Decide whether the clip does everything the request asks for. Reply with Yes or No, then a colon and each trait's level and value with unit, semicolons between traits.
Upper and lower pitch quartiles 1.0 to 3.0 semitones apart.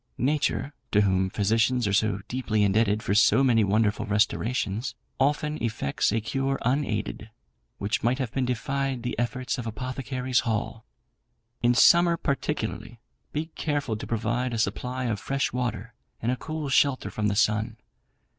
No: average, 3.7 semitones